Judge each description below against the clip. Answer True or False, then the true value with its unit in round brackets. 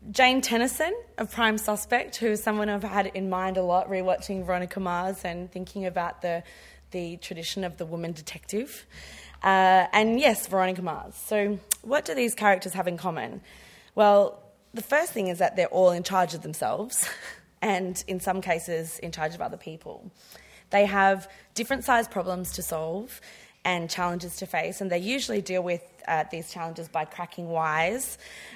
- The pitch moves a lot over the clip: False (3.1 semitones)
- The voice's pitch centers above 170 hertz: True (185 Hz)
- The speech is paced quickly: False (175 wpm)